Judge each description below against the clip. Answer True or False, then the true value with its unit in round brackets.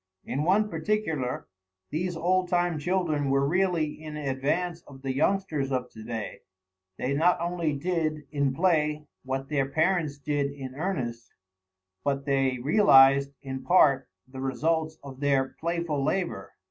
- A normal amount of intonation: True (4.1 semitones)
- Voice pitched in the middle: True (150 Hz)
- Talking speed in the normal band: True (145 wpm)